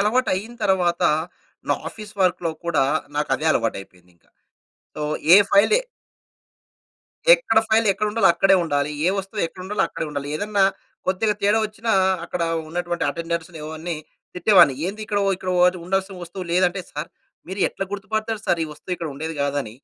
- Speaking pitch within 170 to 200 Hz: Yes, medium, 185 Hz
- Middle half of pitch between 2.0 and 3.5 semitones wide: No, average, 4.1 semitones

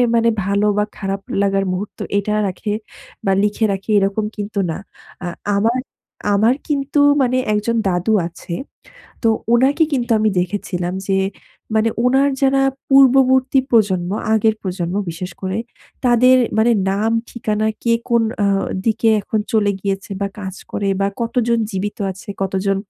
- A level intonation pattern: No, average, 3.3 semitones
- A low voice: No, high, 210 Hz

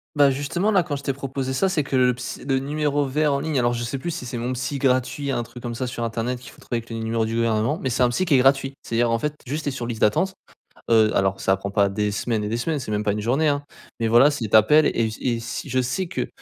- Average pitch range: Yes, average, 3.6 semitones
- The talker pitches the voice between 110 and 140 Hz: Yes, low, 125 Hz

